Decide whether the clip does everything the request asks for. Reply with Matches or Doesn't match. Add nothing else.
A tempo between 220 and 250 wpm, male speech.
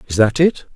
Matches